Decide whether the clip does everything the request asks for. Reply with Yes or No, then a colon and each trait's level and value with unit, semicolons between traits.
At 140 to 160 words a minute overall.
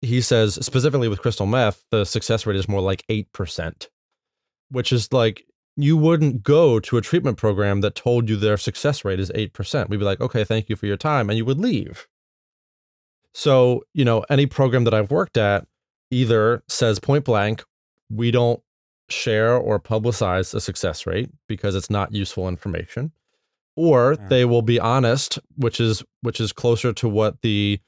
No: average, 180 wpm